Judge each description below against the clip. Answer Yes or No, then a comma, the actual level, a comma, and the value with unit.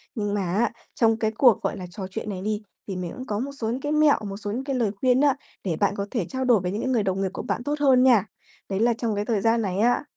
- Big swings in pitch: No, average, 3.9 semitones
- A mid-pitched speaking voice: No, high, 220 Hz